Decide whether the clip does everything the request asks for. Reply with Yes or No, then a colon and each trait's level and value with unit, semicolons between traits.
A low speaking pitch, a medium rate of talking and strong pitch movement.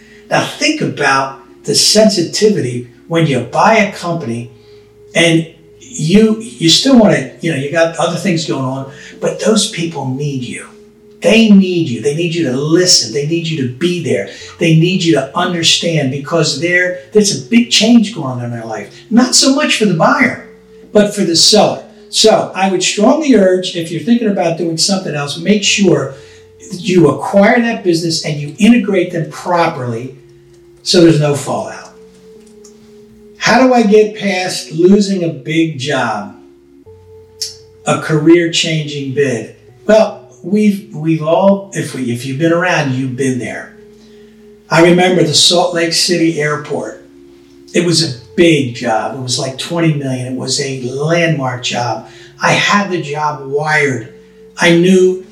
No: medium, 170 Hz; average, 160 wpm; wide, 6.8 semitones